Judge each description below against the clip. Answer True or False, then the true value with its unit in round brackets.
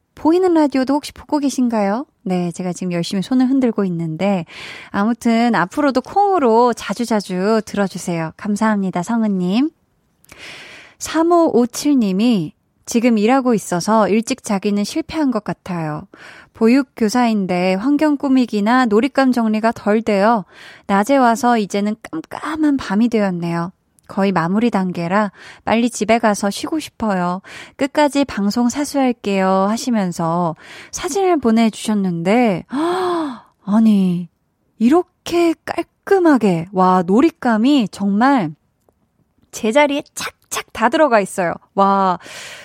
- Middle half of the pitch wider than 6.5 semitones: False (5.5 semitones)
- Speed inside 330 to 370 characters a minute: False (270 characters per minute)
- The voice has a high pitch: True (225 Hz)